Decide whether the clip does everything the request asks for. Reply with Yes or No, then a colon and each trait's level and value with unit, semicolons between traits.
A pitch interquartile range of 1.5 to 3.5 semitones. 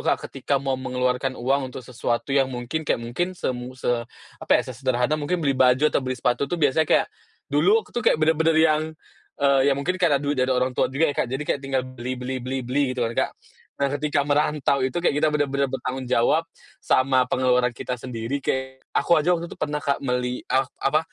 Yes: narrow, 2.5 semitones